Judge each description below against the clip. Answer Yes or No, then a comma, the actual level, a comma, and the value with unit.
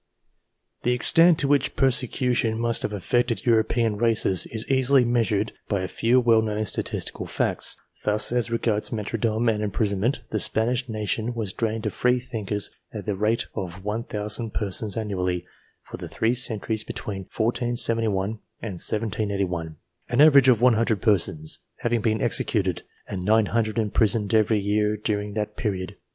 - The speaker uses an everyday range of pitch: No, narrow, 2.3 semitones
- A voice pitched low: Yes, low, 110 Hz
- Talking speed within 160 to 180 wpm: No, average, 150 wpm